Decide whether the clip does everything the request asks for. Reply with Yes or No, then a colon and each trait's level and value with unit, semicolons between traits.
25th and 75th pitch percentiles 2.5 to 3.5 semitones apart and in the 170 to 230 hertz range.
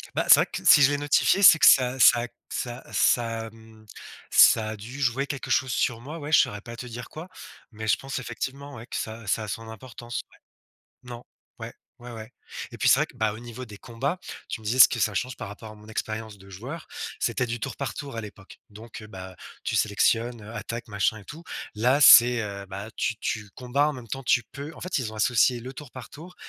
No: average, 3.2 semitones; low, 120 Hz